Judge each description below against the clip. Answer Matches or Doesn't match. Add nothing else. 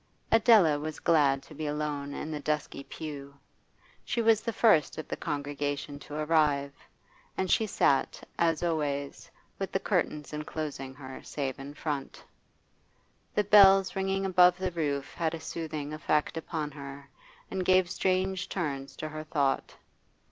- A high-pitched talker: Doesn't match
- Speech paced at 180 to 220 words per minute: Doesn't match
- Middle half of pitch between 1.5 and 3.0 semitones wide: Doesn't match